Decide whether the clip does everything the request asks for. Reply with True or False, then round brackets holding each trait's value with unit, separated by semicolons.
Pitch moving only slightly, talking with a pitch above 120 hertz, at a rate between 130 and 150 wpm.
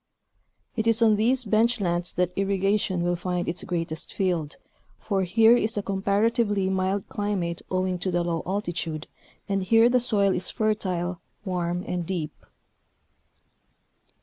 False (3.2 semitones; 190 Hz; 145 wpm)